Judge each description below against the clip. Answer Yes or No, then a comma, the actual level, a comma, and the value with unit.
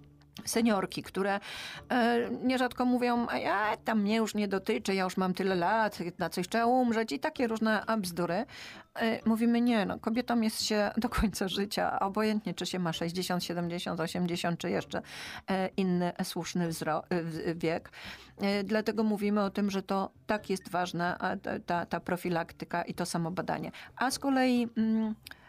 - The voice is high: Yes, high, 200 Hz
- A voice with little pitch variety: No, average, 4.1 semitones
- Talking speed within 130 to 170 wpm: Yes, average, 150 wpm